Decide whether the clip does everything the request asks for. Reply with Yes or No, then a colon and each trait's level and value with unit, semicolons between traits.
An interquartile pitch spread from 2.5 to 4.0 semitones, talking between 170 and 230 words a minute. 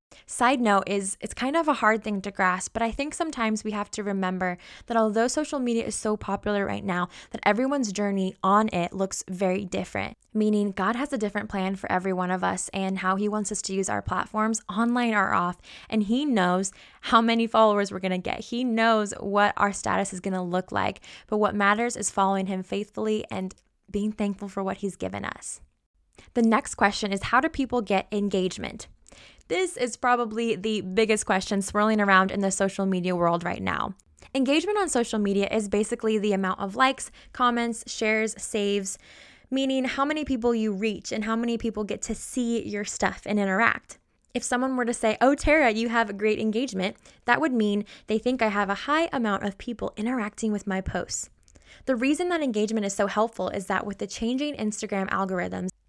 Yes: average, 3.1 semitones; fast, 205 wpm